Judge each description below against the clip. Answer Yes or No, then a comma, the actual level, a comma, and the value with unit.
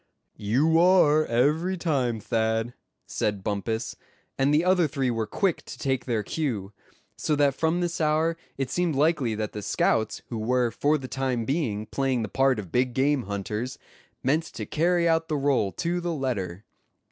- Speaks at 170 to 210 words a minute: Yes, average, 175 wpm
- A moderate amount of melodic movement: No, wide, 5.9 semitones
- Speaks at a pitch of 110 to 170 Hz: Yes, low, 135 Hz